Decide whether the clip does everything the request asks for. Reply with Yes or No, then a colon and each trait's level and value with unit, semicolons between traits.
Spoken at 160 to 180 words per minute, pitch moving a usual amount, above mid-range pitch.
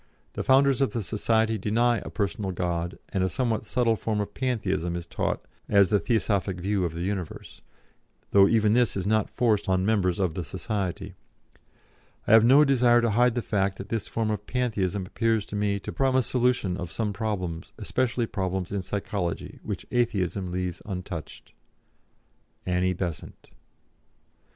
No: average, 165 wpm; average, 3.6 semitones; low, 105 Hz